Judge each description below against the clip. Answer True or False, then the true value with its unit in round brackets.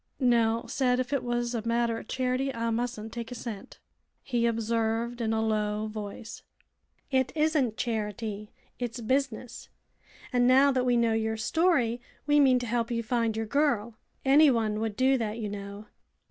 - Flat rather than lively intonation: True (2.3 semitones)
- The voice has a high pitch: True (235 Hz)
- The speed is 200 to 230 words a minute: False (170 wpm)